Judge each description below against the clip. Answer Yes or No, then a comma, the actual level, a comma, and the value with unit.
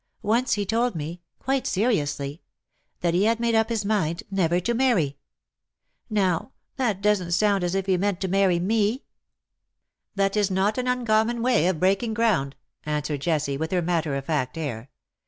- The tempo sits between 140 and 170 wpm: No, average, 180 wpm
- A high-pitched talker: Yes, high, 195 Hz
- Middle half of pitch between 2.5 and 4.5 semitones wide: No, average, 5.2 semitones